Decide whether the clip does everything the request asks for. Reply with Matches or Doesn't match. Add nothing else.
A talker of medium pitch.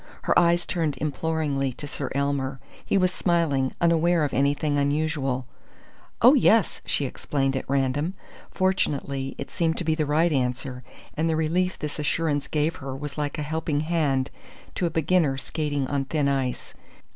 Matches